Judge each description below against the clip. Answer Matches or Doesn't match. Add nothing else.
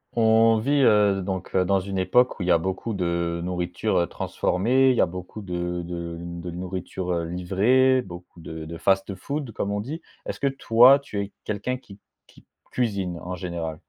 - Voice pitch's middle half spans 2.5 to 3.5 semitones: Doesn't match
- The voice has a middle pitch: Doesn't match